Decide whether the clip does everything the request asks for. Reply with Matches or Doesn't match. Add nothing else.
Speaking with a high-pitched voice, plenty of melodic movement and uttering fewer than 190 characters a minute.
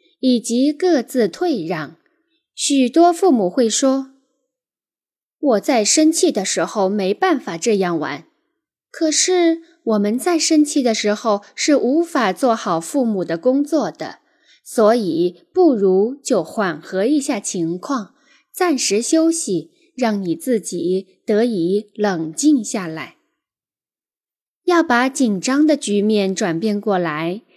Matches